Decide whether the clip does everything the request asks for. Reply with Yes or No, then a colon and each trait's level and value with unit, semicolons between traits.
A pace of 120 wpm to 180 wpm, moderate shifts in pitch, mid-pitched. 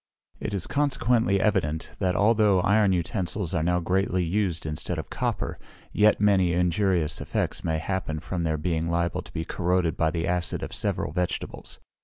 No: average, 170 wpm; average, 3.3 semitones; very low, 90 Hz